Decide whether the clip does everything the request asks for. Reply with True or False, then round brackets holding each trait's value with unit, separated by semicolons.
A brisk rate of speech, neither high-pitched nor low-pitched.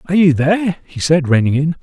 True (230 wpm; 150 Hz)